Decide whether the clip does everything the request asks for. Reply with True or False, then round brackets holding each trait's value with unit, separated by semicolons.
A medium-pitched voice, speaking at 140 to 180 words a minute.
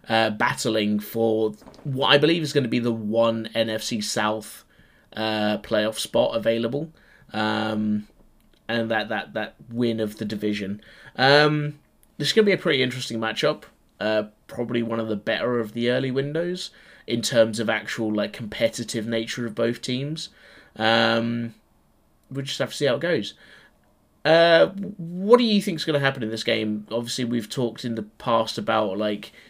False (115 Hz; 175 wpm)